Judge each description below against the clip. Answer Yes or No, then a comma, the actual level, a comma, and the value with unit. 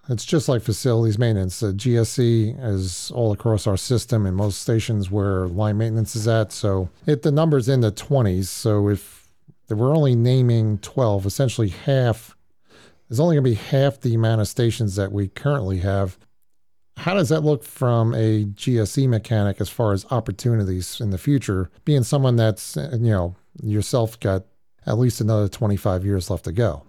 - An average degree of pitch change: Yes, average, 3.6 semitones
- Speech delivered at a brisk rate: No, average, 175 wpm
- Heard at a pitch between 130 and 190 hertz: No, low, 110 Hz